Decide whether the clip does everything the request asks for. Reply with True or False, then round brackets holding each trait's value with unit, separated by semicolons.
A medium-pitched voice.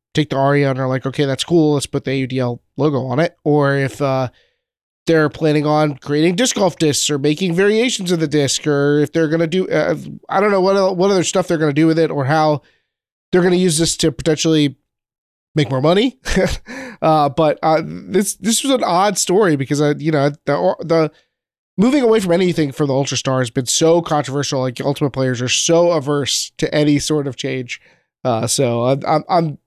True (150 Hz)